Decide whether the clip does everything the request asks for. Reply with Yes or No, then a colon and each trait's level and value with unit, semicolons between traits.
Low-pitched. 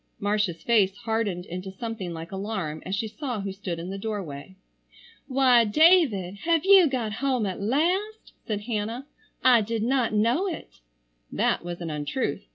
No: high, 215 Hz